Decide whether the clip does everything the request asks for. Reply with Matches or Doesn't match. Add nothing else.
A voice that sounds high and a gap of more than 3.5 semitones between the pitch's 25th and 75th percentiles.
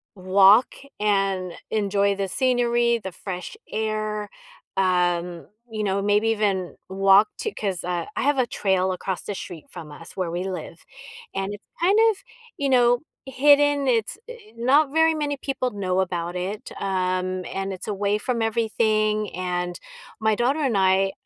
Matches